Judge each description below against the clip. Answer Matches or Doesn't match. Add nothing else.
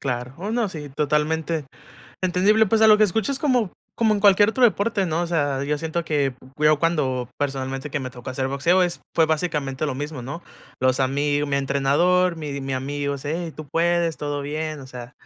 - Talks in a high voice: Doesn't match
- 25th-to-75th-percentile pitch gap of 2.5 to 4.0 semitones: Doesn't match